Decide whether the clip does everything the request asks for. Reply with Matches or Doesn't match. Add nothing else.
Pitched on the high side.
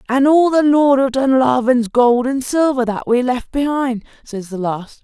Matches